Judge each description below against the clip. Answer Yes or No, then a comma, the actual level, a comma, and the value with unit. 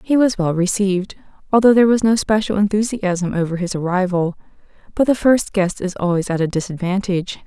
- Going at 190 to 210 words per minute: No, average, 175 wpm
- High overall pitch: Yes, high, 195 Hz